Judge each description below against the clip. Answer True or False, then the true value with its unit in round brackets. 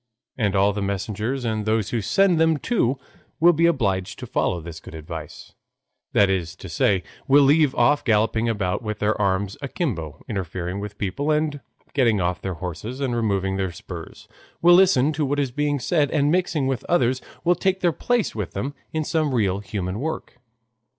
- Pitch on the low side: True (115 Hz)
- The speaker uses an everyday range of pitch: False (7.2 semitones)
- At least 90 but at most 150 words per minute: False (185 wpm)